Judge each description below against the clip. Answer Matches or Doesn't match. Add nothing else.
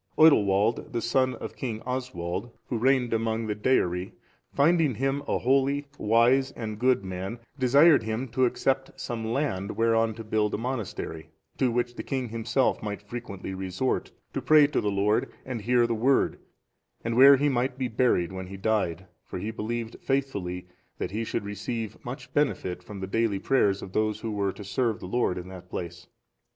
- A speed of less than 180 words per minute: Doesn't match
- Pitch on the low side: Matches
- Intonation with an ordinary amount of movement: Matches